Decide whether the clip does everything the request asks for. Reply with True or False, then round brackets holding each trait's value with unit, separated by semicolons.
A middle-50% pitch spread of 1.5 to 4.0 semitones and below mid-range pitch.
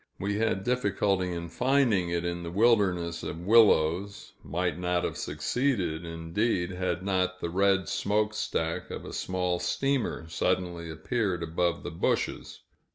True (3.2 semitones; 90 Hz)